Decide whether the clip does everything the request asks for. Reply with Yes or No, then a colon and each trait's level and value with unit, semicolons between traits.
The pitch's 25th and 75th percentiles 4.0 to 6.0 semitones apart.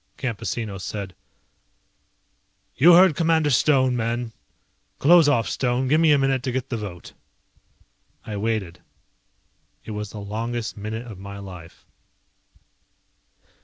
Yes: average, 4.6 semitones